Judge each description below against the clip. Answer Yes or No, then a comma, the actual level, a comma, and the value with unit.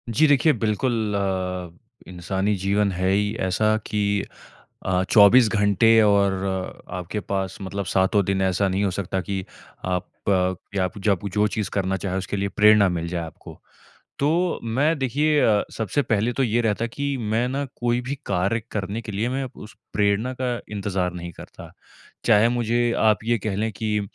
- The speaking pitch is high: No, low, 105 Hz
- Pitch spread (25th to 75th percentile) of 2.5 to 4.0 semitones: Yes, average, 3.3 semitones